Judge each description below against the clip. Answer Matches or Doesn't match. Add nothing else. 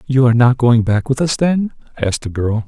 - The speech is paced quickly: Matches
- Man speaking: Matches